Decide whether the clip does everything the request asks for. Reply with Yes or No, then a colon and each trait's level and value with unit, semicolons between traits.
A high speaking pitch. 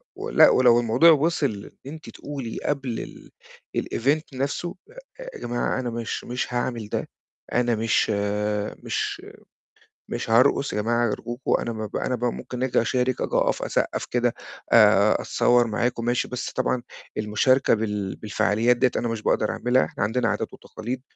No: low, 120 Hz